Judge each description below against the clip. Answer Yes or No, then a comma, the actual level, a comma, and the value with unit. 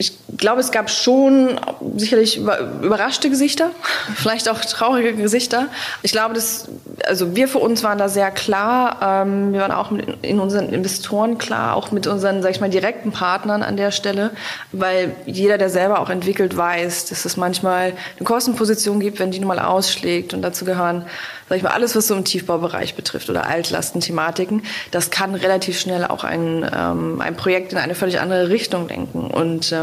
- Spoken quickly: No, average, 175 wpm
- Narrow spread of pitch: No, average, 3.2 semitones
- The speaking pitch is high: Yes, high, 195 Hz